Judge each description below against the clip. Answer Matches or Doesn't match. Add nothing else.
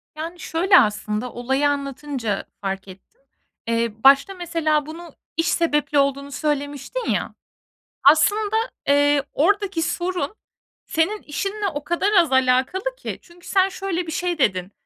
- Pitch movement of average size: Matches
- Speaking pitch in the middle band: Doesn't match